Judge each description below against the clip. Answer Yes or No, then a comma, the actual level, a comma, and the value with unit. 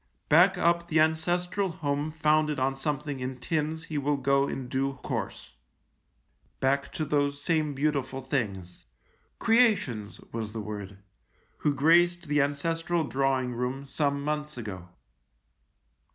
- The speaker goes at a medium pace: Yes, average, 150 wpm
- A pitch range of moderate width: Yes, average, 3.2 semitones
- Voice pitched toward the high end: No, medium, 145 Hz